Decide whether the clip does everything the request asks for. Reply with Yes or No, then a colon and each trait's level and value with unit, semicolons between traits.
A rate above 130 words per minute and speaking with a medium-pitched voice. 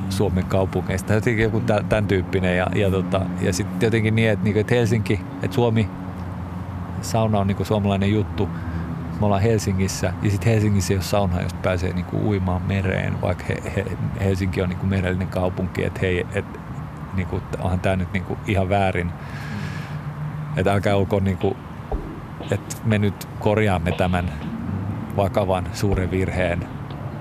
No: average, 150 wpm; very low, 95 Hz